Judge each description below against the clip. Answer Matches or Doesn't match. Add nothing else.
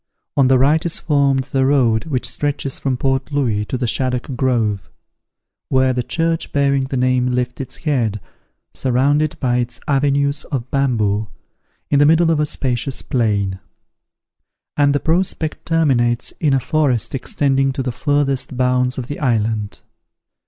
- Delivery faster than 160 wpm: Doesn't match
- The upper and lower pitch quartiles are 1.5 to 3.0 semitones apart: Matches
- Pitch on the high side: Doesn't match